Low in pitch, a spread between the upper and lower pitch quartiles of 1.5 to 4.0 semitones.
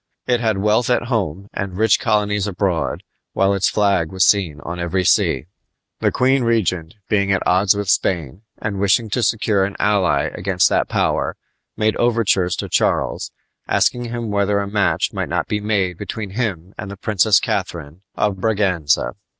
Yes: low, 100 Hz; average, 2.7 semitones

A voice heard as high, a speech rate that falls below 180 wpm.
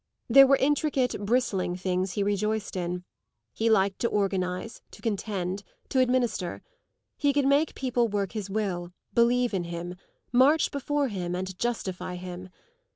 Yes: high, 205 Hz; average, 150 wpm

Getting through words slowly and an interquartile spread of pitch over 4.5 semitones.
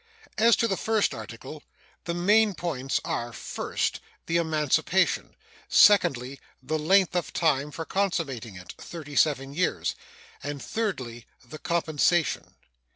Yes: slow, 125 wpm; average, 5.2 semitones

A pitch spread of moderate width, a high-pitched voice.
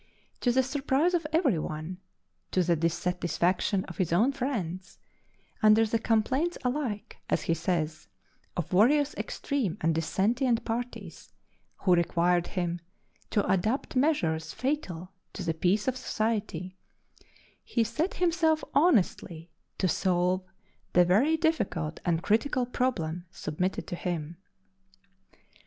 No: wide, 6.9 semitones; high, 200 Hz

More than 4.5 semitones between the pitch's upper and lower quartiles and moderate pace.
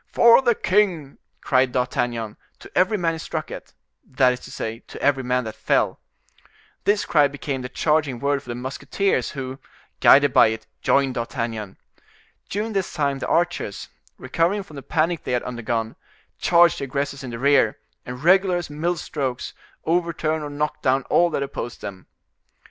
Yes: average, 5.1 semitones; average, 175 wpm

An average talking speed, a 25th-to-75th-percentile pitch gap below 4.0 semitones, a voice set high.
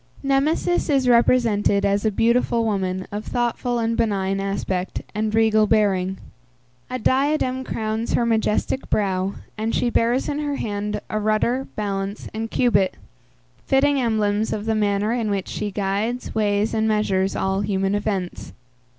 Yes: average, 150 wpm; average, 2.9 semitones; high, 215 Hz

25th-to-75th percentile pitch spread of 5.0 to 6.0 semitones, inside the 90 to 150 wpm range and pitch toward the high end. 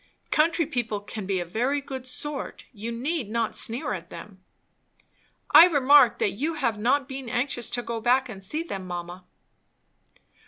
No: average, 5.3 semitones; average, 165 wpm; high, 240 Hz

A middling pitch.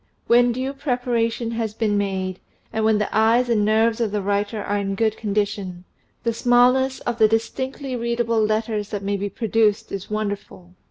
No: high, 220 Hz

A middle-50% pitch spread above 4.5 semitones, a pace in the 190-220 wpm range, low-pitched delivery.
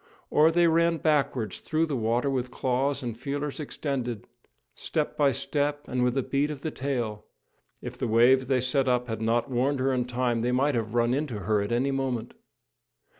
No: average, 2.9 semitones; average, 195 wpm; low, 130 Hz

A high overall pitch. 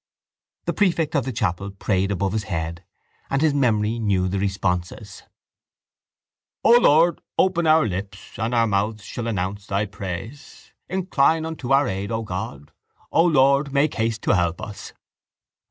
No: low, 110 Hz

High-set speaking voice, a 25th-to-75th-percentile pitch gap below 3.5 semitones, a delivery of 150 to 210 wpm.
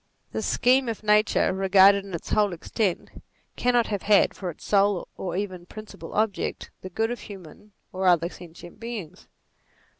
Yes: high, 200 Hz; average, 3.0 semitones; average, 160 wpm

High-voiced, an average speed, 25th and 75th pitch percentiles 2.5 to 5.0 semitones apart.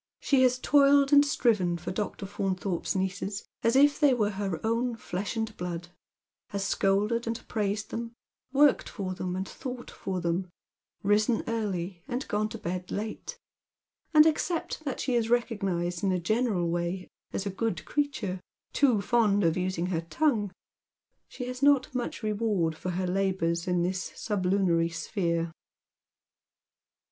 Yes: high, 200 Hz; average, 155 wpm; average, 4.6 semitones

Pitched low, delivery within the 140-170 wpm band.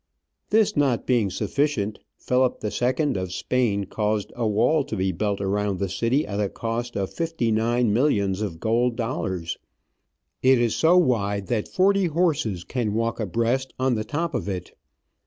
Yes: low, 115 Hz; average, 165 wpm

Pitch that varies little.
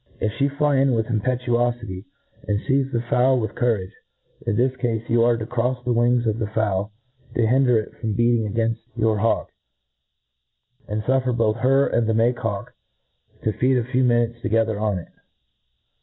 Yes: narrow, 2.2 semitones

